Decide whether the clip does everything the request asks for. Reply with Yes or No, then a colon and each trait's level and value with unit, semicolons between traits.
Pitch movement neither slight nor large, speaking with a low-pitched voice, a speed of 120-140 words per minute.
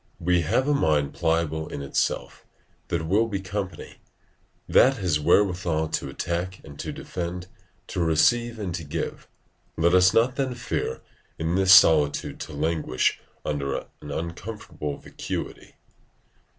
Yes: average, 3.4 semitones; very low, 85 Hz; slow, 135 wpm